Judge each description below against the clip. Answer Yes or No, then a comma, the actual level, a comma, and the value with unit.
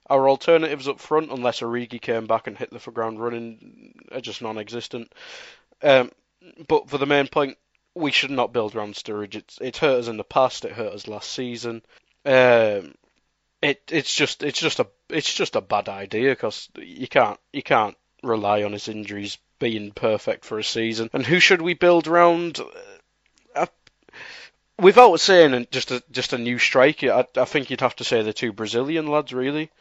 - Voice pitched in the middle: No, low, 125 Hz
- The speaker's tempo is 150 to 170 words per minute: No, average, 185 wpm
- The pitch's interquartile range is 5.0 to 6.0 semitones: Yes, wide, 5.4 semitones